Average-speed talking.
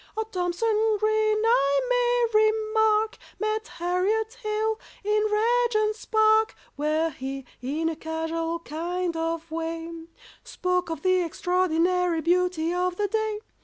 No: slow, 125 wpm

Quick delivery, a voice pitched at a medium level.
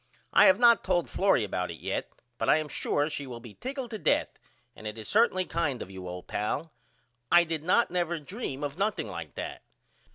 Yes: fast, 215 wpm; medium, 155 Hz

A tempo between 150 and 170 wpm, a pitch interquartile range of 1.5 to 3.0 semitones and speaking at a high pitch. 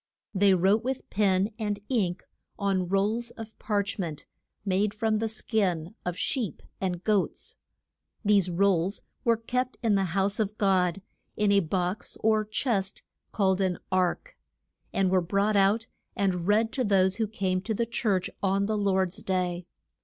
Yes: average, 160 wpm; narrow, 2.6 semitones; high, 200 Hz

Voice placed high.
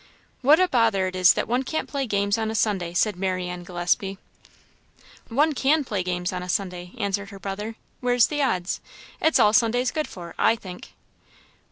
Yes: high, 200 Hz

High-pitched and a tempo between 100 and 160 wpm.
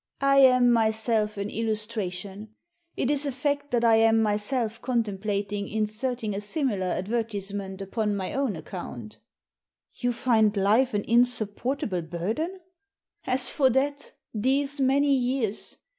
Yes: high, 225 Hz; average, 140 wpm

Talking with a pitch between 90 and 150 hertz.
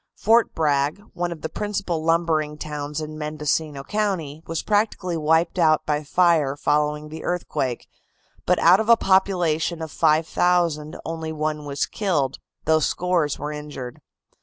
No: medium, 160 Hz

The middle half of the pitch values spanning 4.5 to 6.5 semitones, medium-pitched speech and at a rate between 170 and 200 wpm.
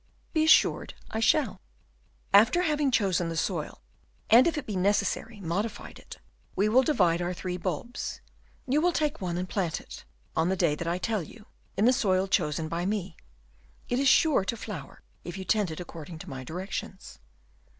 No: average, 5.2 semitones; high, 195 Hz; average, 190 wpm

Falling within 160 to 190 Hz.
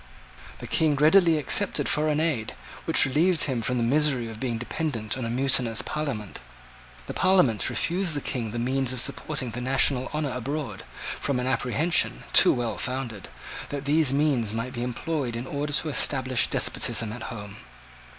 No: low, 130 Hz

